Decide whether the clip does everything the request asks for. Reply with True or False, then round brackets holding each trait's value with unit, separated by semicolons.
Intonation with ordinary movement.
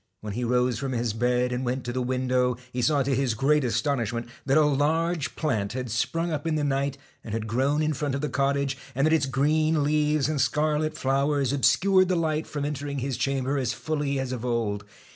True (3.3 semitones)